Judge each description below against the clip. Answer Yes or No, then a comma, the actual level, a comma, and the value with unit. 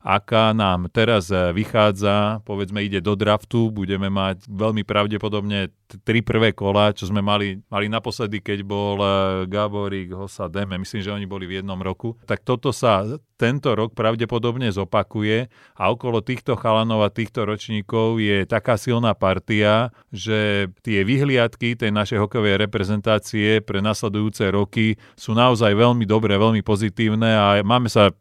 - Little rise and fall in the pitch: Yes, narrow, 2.0 semitones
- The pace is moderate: Yes, average, 150 wpm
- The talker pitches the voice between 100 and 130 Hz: Yes, low, 105 Hz